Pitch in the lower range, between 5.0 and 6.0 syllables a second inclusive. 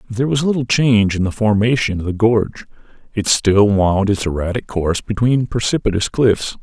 Yes: low, 110 Hz; 5.4 syllables/s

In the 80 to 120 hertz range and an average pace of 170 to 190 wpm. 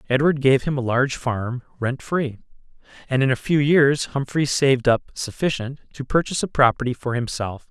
No: low, 135 Hz; average, 180 wpm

